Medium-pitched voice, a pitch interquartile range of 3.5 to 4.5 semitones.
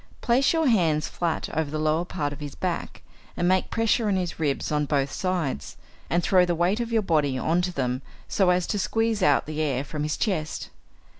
Yes: medium, 170 Hz; average, 4.2 semitones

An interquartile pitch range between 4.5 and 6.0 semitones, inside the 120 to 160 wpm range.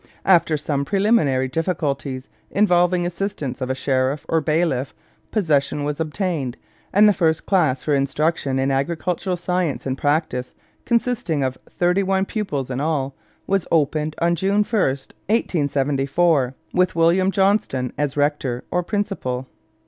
Yes: average, 5.0 semitones; average, 140 wpm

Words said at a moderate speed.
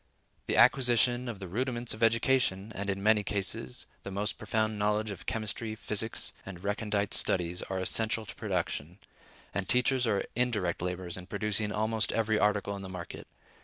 Yes: average, 165 wpm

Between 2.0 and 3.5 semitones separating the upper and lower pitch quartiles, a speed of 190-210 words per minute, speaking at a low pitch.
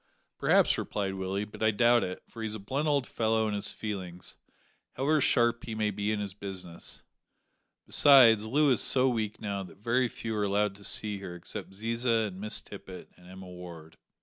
Yes: average, 3.2 semitones; average, 195 wpm; low, 105 Hz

